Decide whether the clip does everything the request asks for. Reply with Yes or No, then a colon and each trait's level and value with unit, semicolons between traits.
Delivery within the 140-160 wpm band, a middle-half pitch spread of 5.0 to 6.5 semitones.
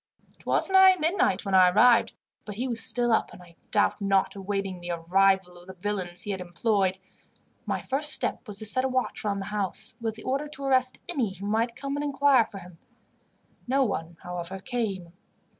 No: fast, 205 wpm; average, 5.3 semitones